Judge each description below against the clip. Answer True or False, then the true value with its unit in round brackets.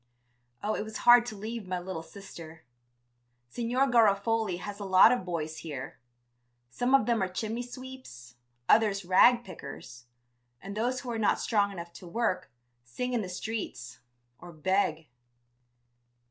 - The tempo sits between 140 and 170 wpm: True (150 wpm)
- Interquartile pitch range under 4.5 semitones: False (5.2 semitones)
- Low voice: False (200 Hz)